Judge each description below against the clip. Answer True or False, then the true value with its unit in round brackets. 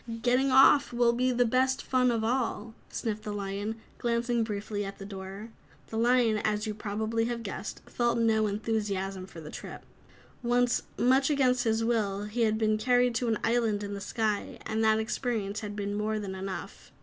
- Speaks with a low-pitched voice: False (220 Hz)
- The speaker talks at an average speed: True (185 wpm)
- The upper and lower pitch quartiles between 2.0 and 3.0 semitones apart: True (2.6 semitones)